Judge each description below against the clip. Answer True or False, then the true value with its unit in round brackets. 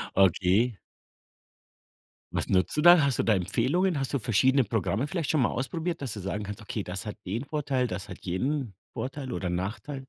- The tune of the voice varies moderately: False (6.1 semitones)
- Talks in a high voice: False (120 Hz)